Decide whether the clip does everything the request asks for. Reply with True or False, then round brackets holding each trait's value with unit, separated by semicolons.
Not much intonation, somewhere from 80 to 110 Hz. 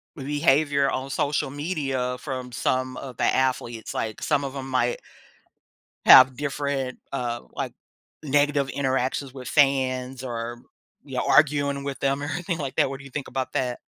False (1.8 semitones; 135 Hz)